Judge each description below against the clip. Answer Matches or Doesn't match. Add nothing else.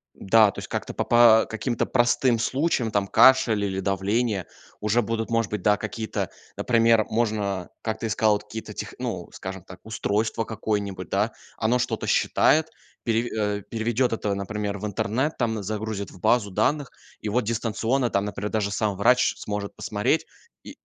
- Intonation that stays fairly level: Matches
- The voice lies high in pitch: Doesn't match